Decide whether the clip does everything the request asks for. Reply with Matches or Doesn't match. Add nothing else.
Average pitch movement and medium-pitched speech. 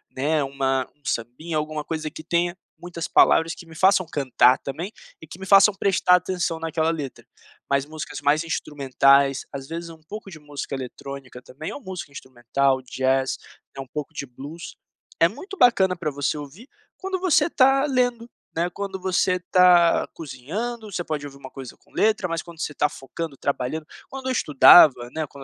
Matches